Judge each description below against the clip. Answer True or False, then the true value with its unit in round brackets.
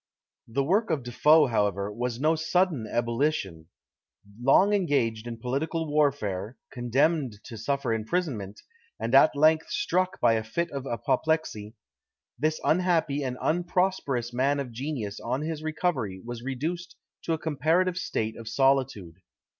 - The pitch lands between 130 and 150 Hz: True (140 Hz)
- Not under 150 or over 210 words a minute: False (140 wpm)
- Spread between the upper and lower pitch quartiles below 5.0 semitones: False (5.6 semitones)